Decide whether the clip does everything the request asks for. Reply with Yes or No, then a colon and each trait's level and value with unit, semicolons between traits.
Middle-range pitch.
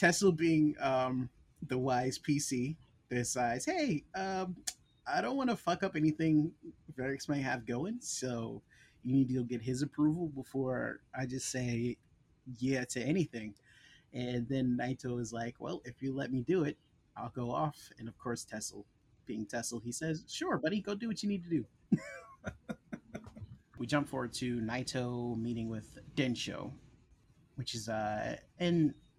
No: low, 130 Hz